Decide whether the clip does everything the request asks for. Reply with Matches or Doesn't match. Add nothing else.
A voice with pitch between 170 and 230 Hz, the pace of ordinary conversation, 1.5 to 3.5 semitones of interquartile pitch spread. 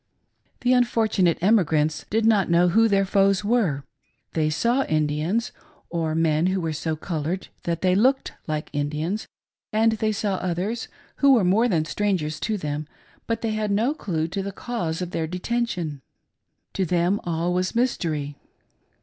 Doesn't match